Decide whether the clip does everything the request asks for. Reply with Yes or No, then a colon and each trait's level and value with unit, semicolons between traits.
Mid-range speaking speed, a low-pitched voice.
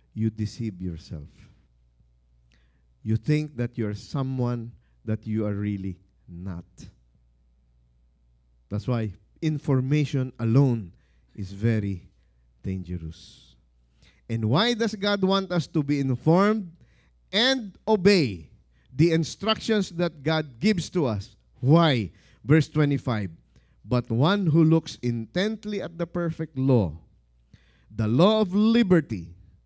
No: slow, 110 wpm; low, 115 Hz